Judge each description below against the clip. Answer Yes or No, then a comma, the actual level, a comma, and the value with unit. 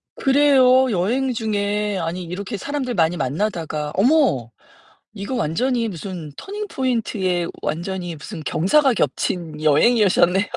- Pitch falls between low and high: No, high, 200 Hz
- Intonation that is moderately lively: No, wide, 6.8 semitones